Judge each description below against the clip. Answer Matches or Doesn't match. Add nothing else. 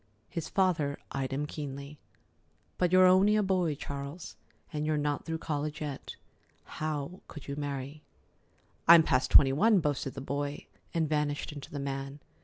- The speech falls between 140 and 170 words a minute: Matches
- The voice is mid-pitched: Matches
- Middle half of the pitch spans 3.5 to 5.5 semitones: Doesn't match